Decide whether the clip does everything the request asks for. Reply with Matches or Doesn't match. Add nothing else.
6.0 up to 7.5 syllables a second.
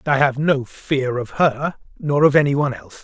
Doesn't match